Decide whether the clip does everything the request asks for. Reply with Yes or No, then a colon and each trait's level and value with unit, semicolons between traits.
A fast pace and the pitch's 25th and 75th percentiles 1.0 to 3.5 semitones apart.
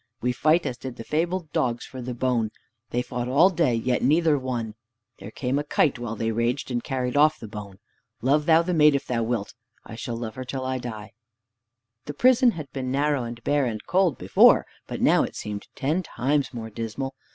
No: fast, 210 wpm; average, 4.0 semitones